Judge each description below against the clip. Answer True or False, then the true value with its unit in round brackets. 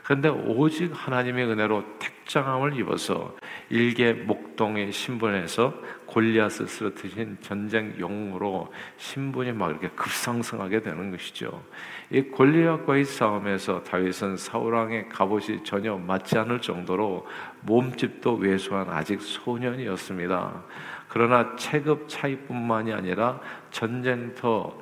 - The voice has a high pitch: False (115 Hz)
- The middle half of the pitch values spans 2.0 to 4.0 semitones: True (3.6 semitones)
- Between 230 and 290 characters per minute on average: True (285 characters per minute)